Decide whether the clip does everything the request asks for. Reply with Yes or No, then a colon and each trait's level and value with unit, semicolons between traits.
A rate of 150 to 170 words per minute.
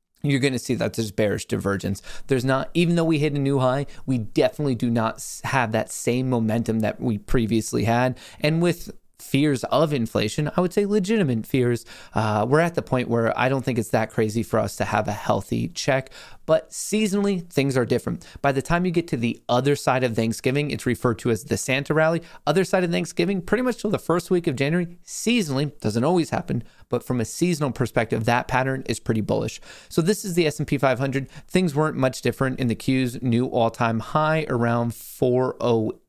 No: fast, 205 wpm